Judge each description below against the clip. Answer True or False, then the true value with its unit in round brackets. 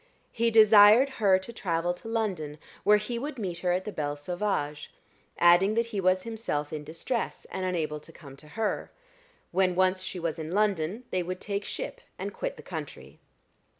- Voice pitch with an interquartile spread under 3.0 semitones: False (4.5 semitones)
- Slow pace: False (185 wpm)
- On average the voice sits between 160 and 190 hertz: True (185 Hz)